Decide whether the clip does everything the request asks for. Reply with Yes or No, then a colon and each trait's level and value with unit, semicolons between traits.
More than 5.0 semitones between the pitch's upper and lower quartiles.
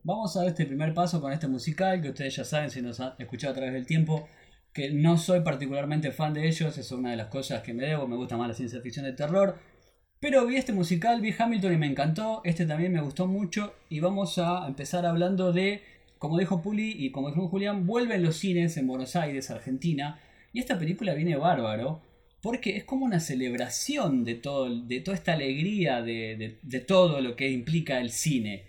Yes: wide, 5.5 semitones